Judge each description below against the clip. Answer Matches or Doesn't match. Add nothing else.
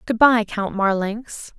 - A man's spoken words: Doesn't match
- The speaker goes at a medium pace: Matches